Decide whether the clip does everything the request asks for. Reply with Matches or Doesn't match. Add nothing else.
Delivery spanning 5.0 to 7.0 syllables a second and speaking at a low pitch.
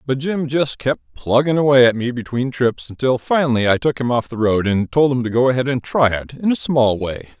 Matches